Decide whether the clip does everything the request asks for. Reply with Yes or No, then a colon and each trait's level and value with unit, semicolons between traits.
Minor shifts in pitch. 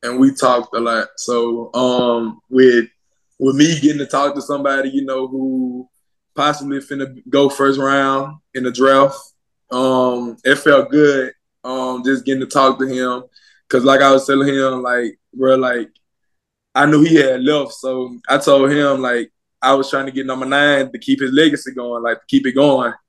Yes: narrow, 1.6 semitones